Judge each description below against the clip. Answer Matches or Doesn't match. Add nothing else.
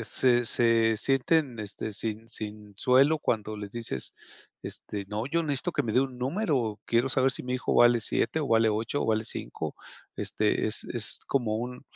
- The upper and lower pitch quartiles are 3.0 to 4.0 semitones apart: Matches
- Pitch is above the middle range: Doesn't match